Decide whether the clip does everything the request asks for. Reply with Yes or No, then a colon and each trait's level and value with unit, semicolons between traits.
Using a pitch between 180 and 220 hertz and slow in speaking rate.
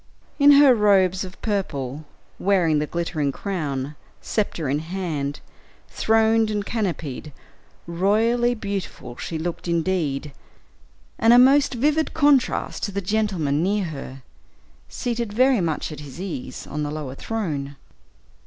Yes: medium, 185 Hz; slow, 130 wpm